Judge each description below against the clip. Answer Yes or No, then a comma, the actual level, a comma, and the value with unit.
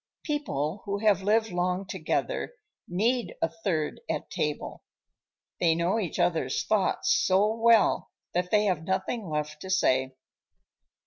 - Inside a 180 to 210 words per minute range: No, slow, 135 wpm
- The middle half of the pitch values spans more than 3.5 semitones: Yes, average, 4.5 semitones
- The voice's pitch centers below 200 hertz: Yes, medium, 185 Hz